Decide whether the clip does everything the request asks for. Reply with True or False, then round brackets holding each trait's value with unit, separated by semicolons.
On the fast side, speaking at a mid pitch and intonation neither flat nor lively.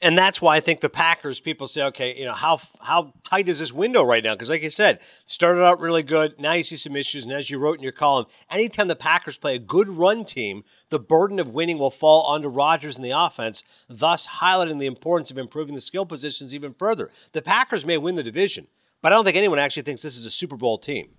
True (250 wpm; 155 Hz; 3.8 semitones)